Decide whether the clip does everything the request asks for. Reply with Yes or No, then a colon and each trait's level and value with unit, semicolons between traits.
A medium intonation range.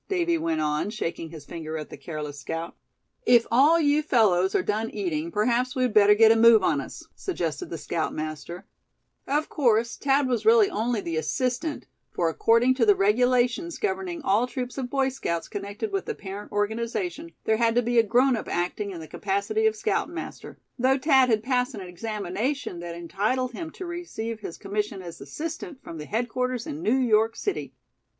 No: wide, 6.3 semitones